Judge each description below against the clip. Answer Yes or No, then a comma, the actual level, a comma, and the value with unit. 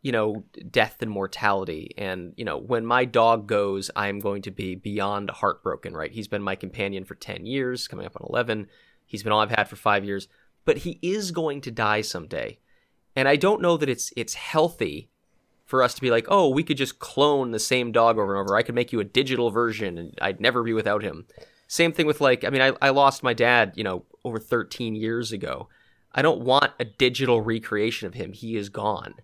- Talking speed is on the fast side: Yes, fast, 230 wpm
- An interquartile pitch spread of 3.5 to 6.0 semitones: Yes, average, 4.1 semitones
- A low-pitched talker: Yes, low, 115 Hz